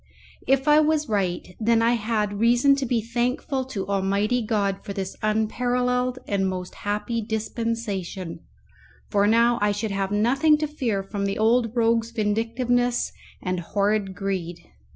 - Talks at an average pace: Yes, average, 150 wpm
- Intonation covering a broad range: No, average, 3.4 semitones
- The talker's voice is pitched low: No, high, 220 Hz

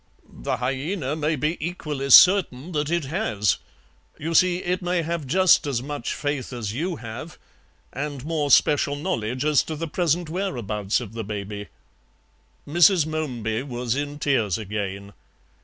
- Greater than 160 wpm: No, average, 150 wpm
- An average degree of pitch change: No, wide, 5.7 semitones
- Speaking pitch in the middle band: Yes, medium, 145 Hz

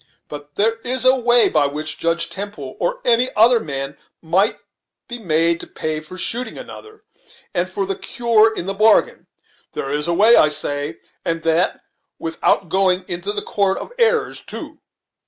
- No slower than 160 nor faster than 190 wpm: Yes, average, 175 wpm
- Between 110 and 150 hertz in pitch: No, medium, 185 Hz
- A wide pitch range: Yes, wide, 6.0 semitones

